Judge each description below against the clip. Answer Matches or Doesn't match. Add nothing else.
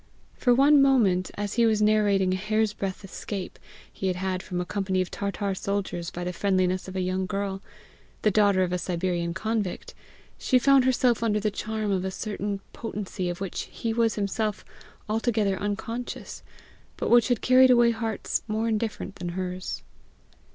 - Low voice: Doesn't match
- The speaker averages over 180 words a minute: Doesn't match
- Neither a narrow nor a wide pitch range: Matches